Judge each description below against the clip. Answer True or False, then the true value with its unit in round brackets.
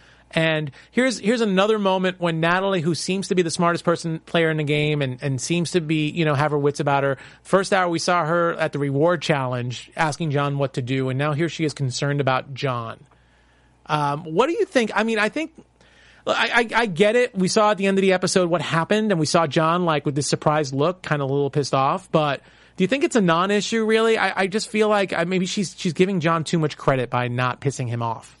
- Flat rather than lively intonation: False (4.9 semitones)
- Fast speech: True (245 wpm)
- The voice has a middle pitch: True (165 Hz)